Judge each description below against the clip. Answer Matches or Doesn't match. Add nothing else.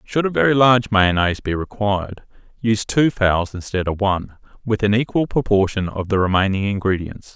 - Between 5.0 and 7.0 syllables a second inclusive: Matches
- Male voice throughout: Matches